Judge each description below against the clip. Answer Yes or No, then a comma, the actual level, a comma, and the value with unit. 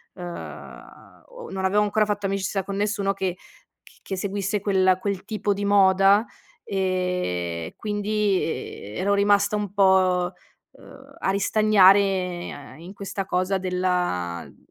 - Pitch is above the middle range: Yes, high, 195 Hz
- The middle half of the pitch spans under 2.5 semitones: Yes, narrow, 1.8 semitones